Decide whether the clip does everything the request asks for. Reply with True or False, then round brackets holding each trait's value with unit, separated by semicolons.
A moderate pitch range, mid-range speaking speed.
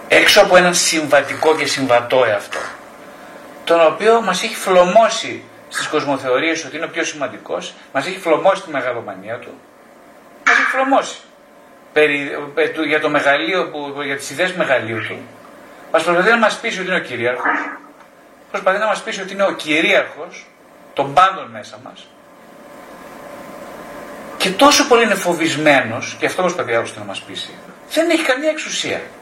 False (5.7 semitones; 155 wpm)